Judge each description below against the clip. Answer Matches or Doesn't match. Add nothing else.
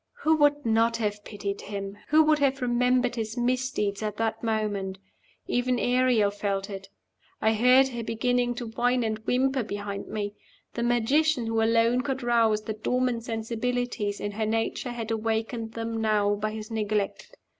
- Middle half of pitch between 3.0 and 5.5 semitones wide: Doesn't match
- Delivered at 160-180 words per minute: Matches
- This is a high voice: Matches